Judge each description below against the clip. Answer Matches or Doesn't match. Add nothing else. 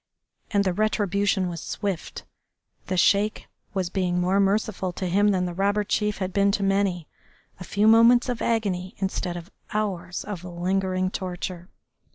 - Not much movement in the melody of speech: Matches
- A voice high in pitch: Matches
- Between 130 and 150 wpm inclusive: Doesn't match